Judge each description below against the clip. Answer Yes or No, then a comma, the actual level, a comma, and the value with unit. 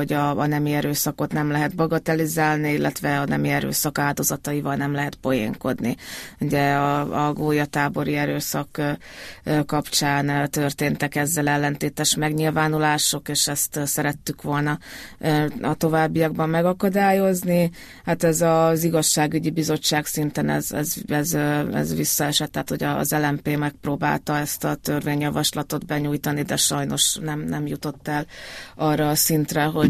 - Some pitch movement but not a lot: No, narrow, 1.1 semitones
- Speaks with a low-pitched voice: No, medium, 150 Hz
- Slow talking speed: No, average, 125 wpm